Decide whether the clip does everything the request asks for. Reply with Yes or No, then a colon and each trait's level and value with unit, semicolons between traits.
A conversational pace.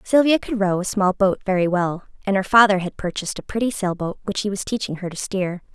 No: fast, 240 wpm